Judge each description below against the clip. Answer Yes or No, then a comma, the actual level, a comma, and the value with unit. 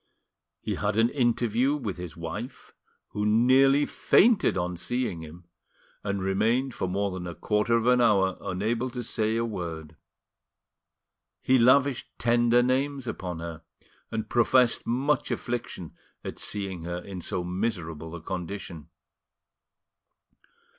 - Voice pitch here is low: Yes, low, 105 Hz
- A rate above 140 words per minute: No, slow, 135 wpm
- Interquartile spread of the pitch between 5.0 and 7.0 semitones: Yes, wide, 5.4 semitones